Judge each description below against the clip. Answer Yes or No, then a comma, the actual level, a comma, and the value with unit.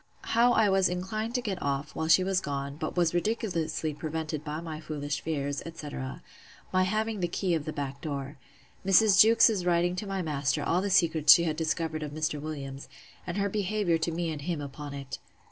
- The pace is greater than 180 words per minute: Yes, average, 200 wpm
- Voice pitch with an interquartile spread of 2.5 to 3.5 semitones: No, average, 4.2 semitones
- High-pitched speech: No, medium, 165 Hz